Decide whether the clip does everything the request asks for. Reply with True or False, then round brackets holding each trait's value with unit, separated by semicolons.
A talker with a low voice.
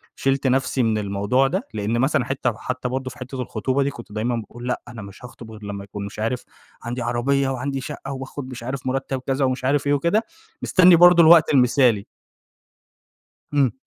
True (130 Hz)